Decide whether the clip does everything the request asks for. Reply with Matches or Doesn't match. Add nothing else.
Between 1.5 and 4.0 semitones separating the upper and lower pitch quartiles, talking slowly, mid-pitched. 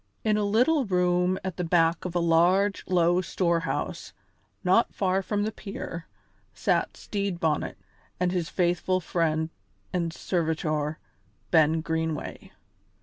Matches